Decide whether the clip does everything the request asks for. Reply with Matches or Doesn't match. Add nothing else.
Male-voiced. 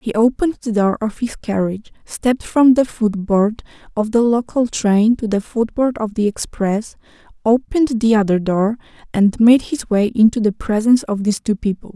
Doesn't match